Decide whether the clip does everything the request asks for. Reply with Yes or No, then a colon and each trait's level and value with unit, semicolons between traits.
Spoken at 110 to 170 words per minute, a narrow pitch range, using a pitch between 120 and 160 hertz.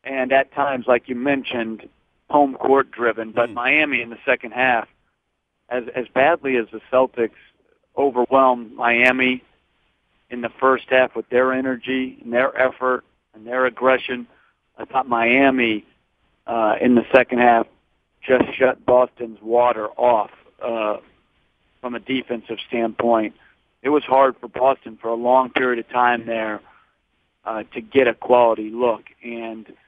Yes: average, 145 wpm; narrow, 1.9 semitones; low, 125 Hz